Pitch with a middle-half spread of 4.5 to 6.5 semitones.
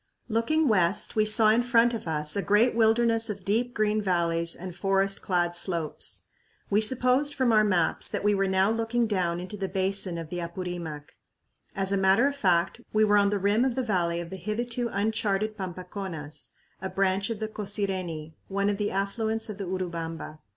No: average, 3.6 semitones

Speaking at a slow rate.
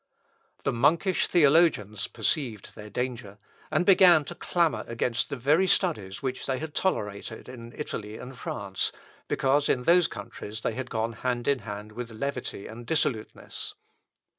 No: average, 150 wpm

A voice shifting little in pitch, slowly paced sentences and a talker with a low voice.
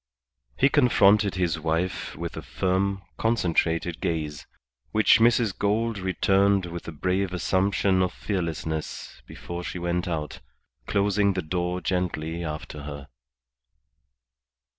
No: average, 3.1 semitones; slow, 120 wpm; very low, 90 Hz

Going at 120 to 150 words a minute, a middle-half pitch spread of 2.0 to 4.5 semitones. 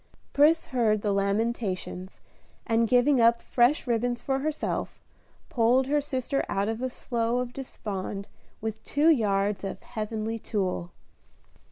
Yes: slow, 135 wpm; average, 3.7 semitones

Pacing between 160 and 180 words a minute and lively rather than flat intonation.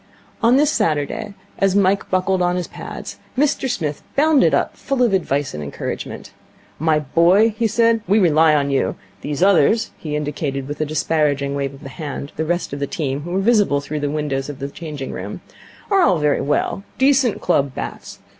No: average, 190 wpm; wide, 6.0 semitones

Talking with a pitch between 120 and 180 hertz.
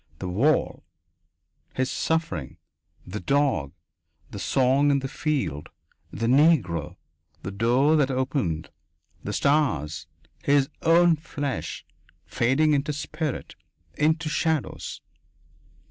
Yes: medium, 140 Hz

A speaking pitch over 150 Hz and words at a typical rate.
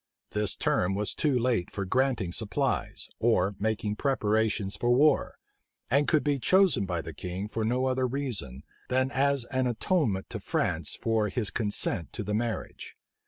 No: low, 115 Hz; average, 165 wpm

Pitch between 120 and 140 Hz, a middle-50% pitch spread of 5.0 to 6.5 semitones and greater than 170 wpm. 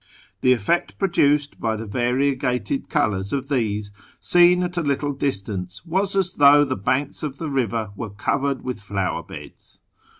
No: low, 135 Hz; average, 5.3 semitones; average, 160 wpm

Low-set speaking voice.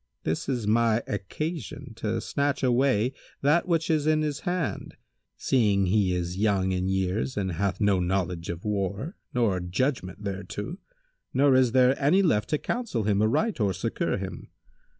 Yes: low, 110 Hz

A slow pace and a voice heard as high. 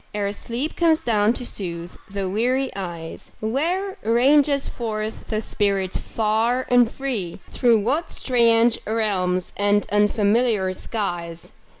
Yes: slow, 120 wpm; high, 220 Hz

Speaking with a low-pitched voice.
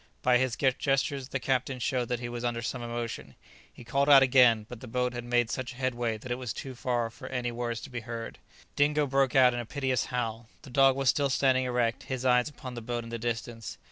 Yes: low, 125 Hz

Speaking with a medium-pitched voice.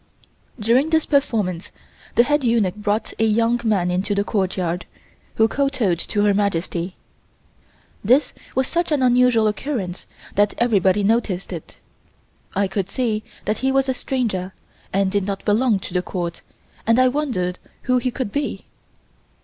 No: high, 215 Hz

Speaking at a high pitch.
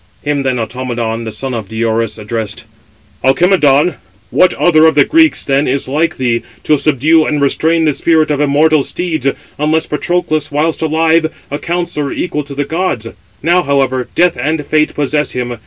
No: medium, 150 Hz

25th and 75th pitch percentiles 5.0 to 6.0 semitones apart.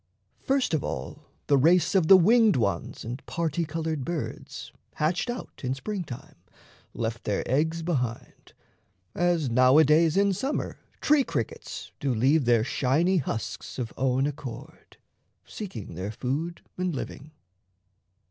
Yes: wide, 5.5 semitones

